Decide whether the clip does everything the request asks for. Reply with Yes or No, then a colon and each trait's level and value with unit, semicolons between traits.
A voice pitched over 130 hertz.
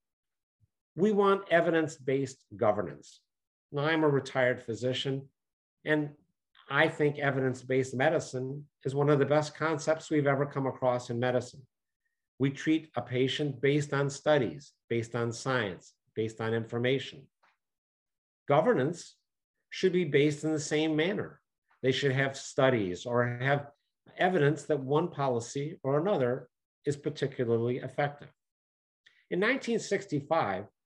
Yes: medium, 140 Hz